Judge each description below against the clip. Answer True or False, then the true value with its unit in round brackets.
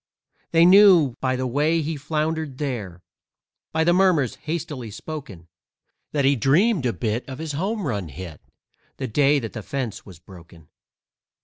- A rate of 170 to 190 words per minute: False (155 wpm)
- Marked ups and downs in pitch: True (6.2 semitones)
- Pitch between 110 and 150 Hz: True (140 Hz)